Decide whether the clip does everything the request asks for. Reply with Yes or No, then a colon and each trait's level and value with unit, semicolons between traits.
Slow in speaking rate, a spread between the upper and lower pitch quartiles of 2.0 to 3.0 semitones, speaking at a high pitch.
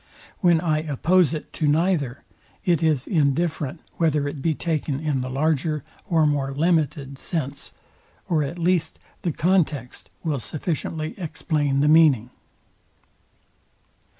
No: slow, 125 wpm; average, 2.7 semitones; medium, 155 Hz